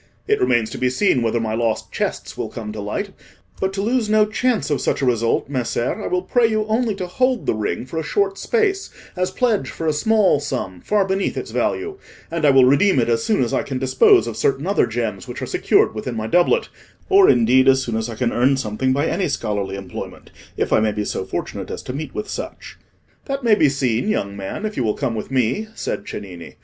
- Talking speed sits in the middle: No, fast, 235 wpm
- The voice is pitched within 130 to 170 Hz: Yes, low, 135 Hz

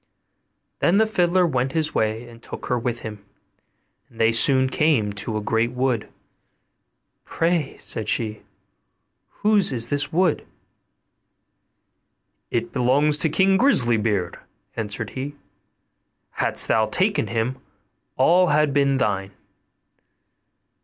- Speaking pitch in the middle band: No, low, 130 Hz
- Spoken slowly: Yes, slow, 120 wpm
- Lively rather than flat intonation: Yes, wide, 5.8 semitones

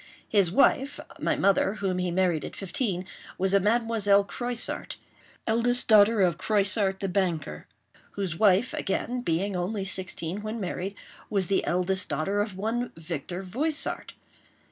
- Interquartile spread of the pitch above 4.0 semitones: No, average, 3.2 semitones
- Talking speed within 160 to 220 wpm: No, slow, 135 wpm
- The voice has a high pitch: Yes, high, 195 Hz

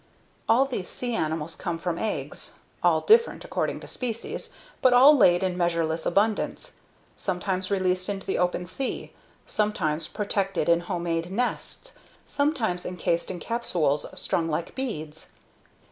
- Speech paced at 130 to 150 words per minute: Yes, slow, 135 wpm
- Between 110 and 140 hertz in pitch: No, medium, 185 Hz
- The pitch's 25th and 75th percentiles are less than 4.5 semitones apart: No, average, 5.0 semitones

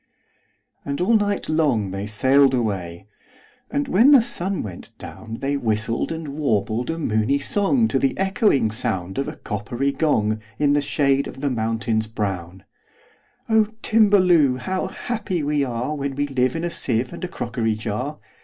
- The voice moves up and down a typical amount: No, wide, 7.1 semitones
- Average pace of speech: Yes, average, 145 wpm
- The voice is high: No, low, 135 Hz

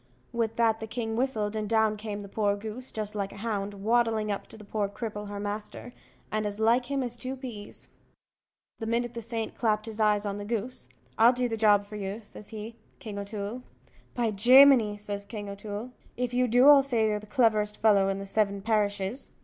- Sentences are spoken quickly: Yes, fast, 210 wpm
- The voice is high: Yes, high, 215 Hz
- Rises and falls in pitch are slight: Yes, narrow, 2.3 semitones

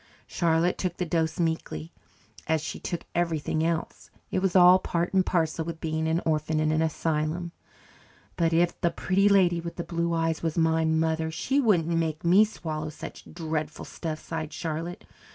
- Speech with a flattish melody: Yes, narrow, 1.5 semitones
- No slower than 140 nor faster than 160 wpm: No, average, 175 wpm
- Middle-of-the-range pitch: Yes, medium, 165 Hz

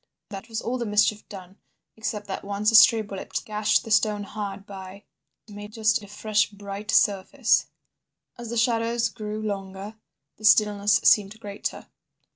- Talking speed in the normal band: Yes, average, 150 wpm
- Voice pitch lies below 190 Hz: No, high, 210 Hz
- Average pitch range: No, narrow, 1.5 semitones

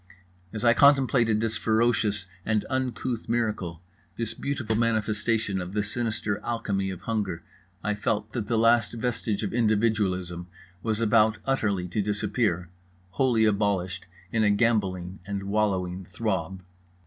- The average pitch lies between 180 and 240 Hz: No, low, 105 Hz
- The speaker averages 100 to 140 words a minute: Yes, slow, 135 wpm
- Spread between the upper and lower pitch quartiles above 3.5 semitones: No, average, 2.9 semitones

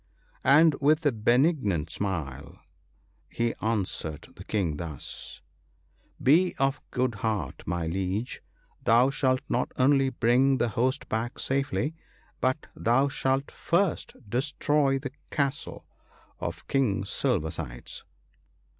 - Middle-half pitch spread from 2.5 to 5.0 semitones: No, wide, 5.4 semitones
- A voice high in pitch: No, low, 125 Hz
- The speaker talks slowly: Yes, slow, 120 wpm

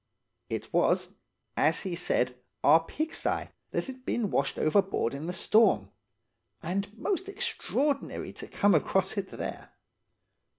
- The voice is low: No, high, 195 Hz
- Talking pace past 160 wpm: No, slow, 135 wpm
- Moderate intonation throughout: No, wide, 8.1 semitones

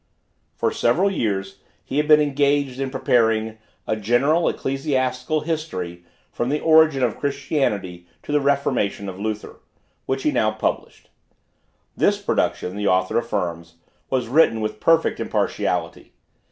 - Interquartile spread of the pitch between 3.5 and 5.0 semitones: No, wide, 5.5 semitones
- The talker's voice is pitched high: No, low, 125 Hz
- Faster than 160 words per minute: No, slow, 135 wpm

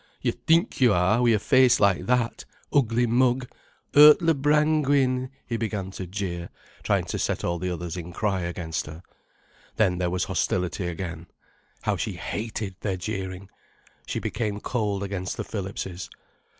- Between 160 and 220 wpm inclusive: No, average, 145 wpm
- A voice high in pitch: No, low, 100 Hz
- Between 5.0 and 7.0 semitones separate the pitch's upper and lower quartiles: Yes, wide, 5.4 semitones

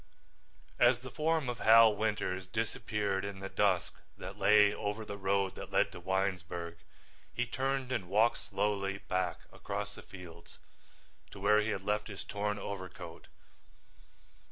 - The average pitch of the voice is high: No, low, 100 Hz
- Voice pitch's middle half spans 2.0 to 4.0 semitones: Yes, narrow, 2.5 semitones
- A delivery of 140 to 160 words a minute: Yes, average, 150 wpm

